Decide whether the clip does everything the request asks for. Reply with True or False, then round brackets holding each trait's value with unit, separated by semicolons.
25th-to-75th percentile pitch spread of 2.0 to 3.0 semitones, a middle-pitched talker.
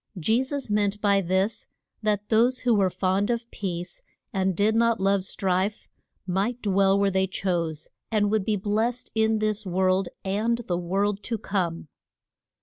False (2.6 semitones; 200 Hz)